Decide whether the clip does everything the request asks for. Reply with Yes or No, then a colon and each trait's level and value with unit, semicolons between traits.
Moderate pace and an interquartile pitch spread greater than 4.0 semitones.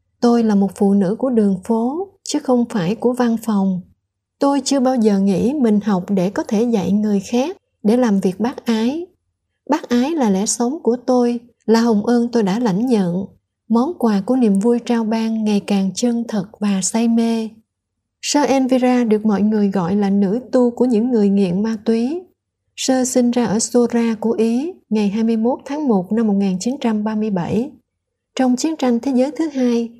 No: average, 190 wpm; average, 2.8 semitones